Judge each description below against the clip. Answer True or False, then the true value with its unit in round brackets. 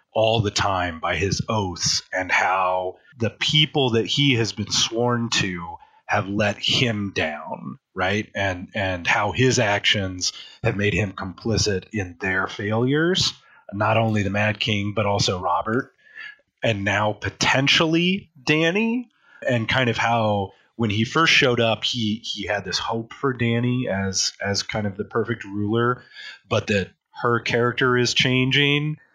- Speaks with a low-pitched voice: True (115 Hz)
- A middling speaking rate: True (150 wpm)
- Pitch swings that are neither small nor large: True (4.1 semitones)